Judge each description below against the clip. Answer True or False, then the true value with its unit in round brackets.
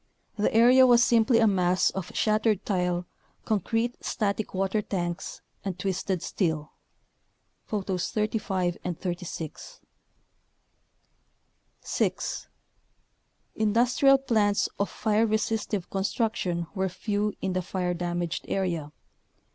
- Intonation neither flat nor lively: True (3.5 semitones)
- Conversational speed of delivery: False (105 wpm)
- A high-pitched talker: True (200 Hz)